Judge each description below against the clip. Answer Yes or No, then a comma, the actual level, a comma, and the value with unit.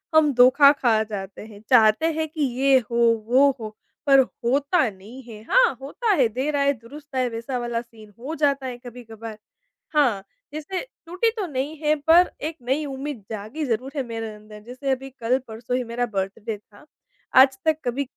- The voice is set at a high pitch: Yes, very high, 255 Hz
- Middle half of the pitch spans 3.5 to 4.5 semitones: Yes, average, 4.1 semitones